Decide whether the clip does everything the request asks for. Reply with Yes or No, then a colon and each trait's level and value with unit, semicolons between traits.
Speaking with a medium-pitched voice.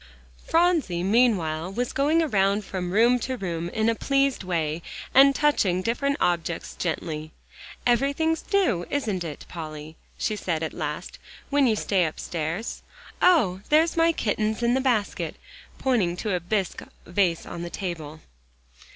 No: high, 200 Hz